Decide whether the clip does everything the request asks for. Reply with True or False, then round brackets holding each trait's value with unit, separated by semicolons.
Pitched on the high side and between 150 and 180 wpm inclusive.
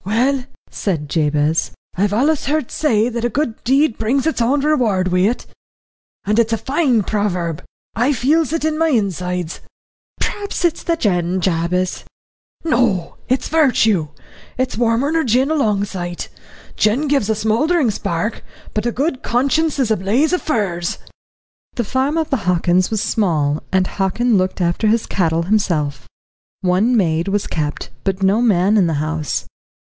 True (215 Hz; 165 wpm)